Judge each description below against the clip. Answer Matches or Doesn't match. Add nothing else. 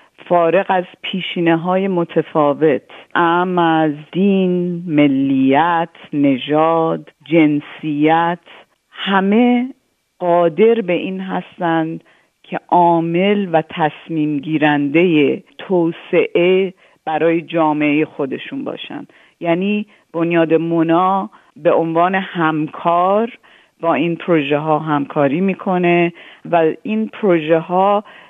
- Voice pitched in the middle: Matches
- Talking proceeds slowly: Matches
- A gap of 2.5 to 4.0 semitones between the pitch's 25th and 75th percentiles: Matches